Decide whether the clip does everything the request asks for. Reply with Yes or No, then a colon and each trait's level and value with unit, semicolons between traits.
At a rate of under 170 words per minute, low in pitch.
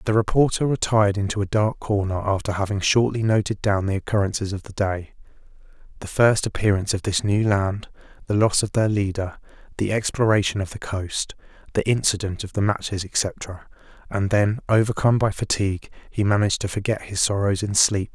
No: average, 175 wpm; low, 100 Hz